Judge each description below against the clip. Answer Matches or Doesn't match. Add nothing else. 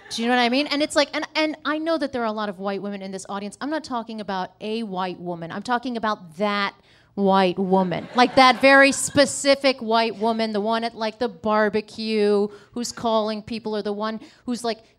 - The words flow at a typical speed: Doesn't match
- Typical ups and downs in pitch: Matches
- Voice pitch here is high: Matches